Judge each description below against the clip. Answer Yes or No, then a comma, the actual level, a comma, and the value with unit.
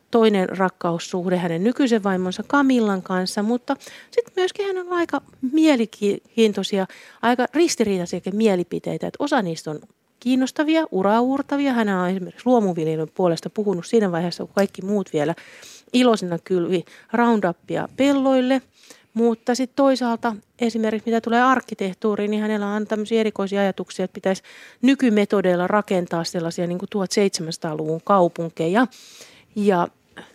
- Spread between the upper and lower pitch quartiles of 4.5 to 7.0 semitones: Yes, average, 4.9 semitones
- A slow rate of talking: No, average, 125 wpm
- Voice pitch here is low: No, high, 210 Hz